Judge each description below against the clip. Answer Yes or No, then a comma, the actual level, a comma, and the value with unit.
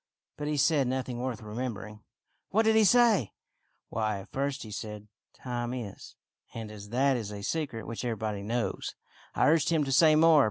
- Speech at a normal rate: No, fast, 210 wpm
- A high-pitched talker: No, low, 125 Hz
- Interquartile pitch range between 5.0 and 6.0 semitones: Yes, wide, 5.6 semitones